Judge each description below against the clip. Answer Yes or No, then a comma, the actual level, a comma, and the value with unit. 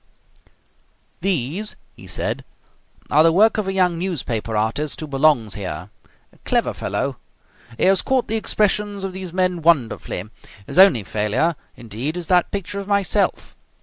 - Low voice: No, medium, 170 Hz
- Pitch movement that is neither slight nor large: No, wide, 7.8 semitones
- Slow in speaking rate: No, average, 150 wpm